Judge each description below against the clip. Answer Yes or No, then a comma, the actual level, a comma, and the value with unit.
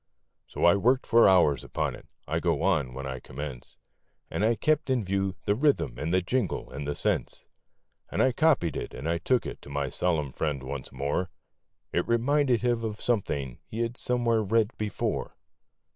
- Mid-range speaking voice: No, very low, 95 Hz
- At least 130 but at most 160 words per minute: No, average, 185 wpm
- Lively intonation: Yes, wide, 8.6 semitones